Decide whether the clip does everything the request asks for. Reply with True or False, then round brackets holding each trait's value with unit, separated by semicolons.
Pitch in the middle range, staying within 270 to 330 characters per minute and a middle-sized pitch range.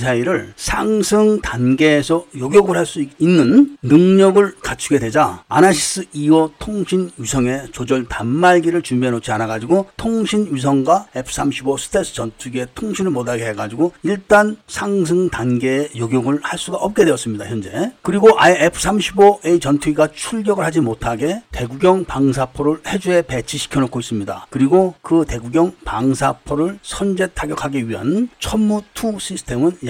False (155 Hz; 320 characters per minute; 6.7 semitones)